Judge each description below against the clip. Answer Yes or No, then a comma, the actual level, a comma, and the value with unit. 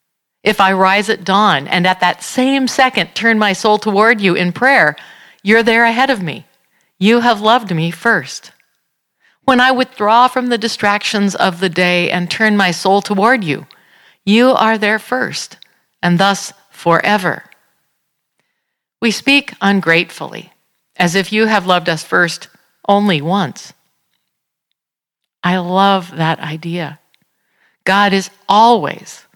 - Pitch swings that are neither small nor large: Yes, average, 4.1 semitones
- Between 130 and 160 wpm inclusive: Yes, average, 140 wpm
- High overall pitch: Yes, high, 200 Hz